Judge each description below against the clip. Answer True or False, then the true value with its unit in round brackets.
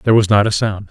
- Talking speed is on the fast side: True (330 wpm)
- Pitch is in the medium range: False (105 Hz)